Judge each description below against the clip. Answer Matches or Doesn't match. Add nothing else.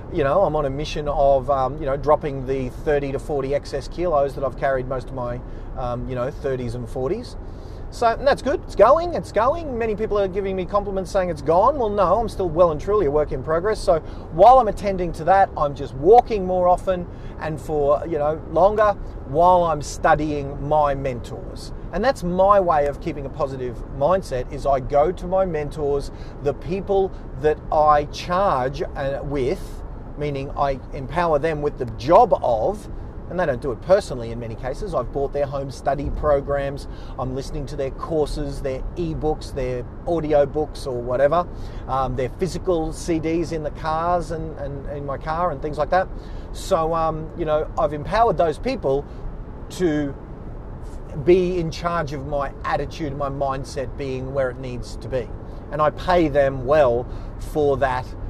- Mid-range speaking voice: Matches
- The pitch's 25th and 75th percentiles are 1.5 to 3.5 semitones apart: Doesn't match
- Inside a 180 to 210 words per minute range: Matches